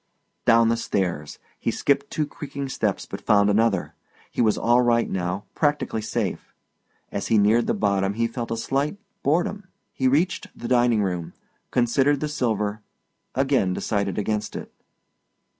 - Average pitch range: Yes, average, 4.7 semitones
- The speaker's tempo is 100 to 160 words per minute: Yes, average, 155 wpm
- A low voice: Yes, low, 115 Hz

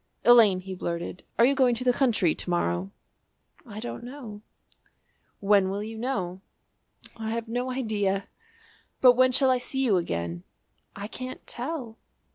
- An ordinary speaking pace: Yes, average, 155 wpm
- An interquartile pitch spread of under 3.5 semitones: No, average, 4.8 semitones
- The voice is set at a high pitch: Yes, high, 225 Hz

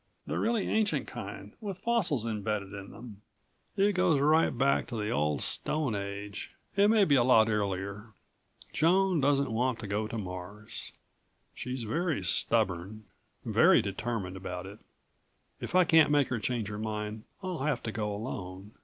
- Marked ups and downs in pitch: Yes, wide, 6.9 semitones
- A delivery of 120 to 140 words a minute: No, average, 160 wpm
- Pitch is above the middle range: No, low, 115 Hz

